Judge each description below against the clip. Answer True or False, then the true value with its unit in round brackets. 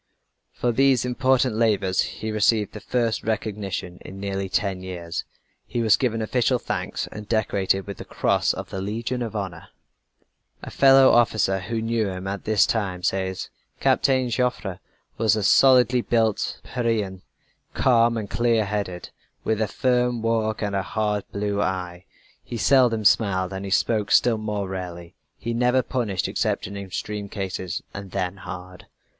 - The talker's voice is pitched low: True (105 Hz)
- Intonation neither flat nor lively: True (3.4 semitones)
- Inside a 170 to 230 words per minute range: False (160 wpm)